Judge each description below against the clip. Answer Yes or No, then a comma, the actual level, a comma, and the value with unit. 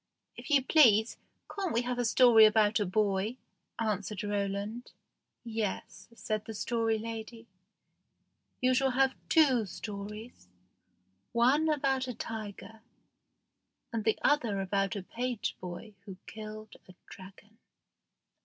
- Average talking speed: No, slow, 125 wpm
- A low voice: No, high, 220 Hz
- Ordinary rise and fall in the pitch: Yes, average, 3.1 semitones